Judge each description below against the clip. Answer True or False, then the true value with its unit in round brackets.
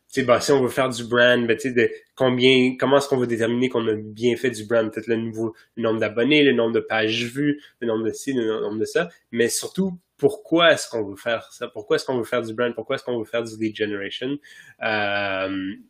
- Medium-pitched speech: False (120 Hz)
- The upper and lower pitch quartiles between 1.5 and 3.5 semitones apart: True (3.1 semitones)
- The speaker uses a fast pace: True (240 wpm)